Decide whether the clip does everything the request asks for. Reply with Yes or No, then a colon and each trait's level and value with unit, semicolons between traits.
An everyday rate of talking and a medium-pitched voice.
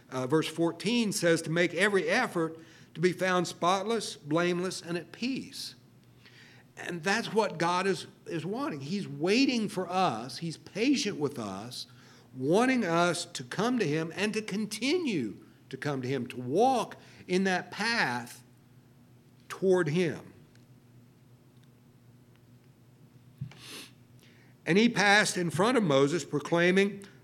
No: slow, 130 wpm; medium, 165 Hz